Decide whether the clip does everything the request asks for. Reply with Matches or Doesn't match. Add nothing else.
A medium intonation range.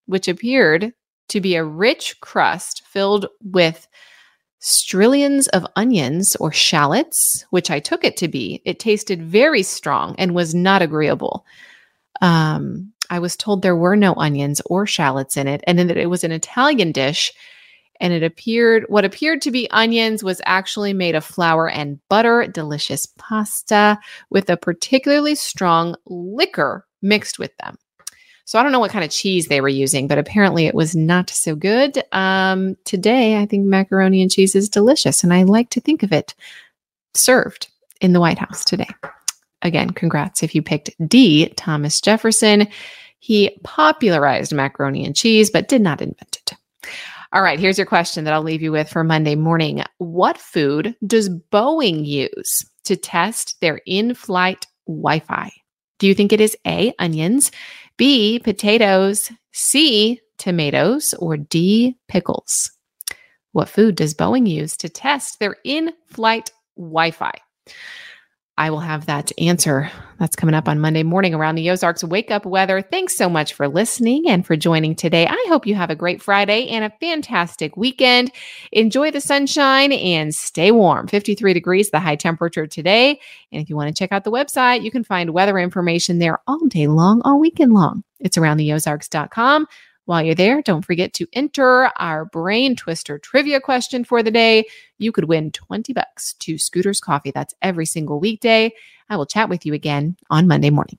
Doesn't match